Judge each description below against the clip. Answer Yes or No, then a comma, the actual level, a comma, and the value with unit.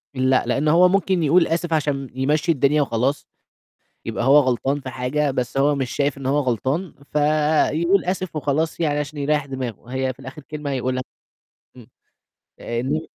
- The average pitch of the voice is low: No, medium, 145 Hz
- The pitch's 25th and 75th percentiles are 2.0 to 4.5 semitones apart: Yes, average, 2.8 semitones